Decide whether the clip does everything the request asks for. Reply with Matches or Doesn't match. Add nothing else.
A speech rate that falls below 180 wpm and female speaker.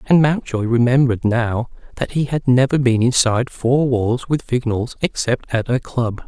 Doesn't match